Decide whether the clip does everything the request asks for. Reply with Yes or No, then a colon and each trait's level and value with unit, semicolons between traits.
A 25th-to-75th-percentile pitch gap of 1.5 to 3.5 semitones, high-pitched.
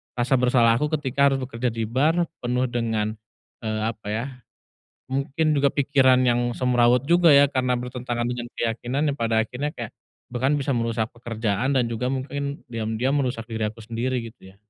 No: average, 2.8 semitones; low, 125 Hz